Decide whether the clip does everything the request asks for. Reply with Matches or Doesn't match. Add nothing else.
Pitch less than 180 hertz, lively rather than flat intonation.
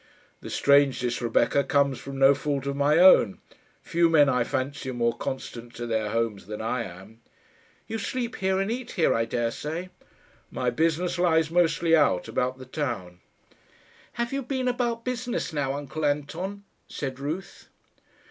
Matches